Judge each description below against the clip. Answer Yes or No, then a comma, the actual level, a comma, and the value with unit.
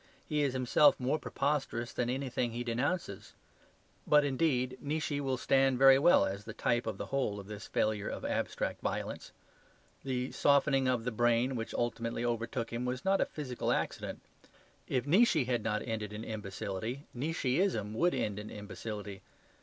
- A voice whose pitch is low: Yes, low, 125 Hz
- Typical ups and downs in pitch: Yes, average, 3.6 semitones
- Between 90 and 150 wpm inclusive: No, average, 165 wpm